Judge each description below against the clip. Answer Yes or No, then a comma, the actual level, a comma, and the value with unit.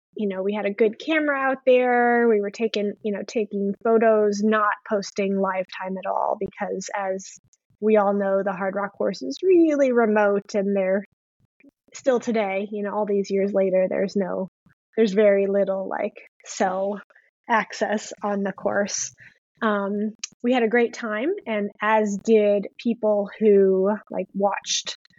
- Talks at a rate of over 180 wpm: No, average, 160 wpm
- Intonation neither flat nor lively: No, narrow, 2.2 semitones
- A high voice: Yes, high, 205 Hz